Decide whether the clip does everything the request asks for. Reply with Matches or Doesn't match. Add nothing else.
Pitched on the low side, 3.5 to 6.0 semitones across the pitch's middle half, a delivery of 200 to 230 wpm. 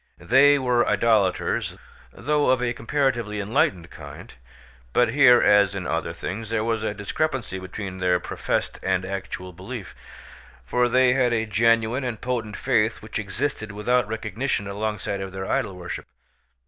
Doesn't match